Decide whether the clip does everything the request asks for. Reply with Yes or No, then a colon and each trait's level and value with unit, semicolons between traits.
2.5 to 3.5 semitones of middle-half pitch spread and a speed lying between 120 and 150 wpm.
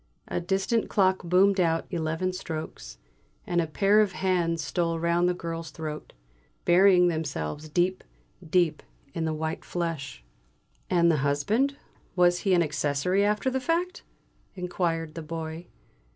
Yes: average, 2.8 semitones; average, 140 wpm